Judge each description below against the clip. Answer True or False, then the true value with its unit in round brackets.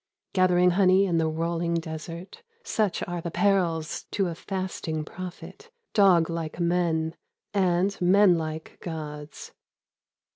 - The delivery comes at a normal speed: False (125 wpm)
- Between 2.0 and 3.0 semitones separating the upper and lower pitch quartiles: True (2.5 semitones)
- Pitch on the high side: False (175 Hz)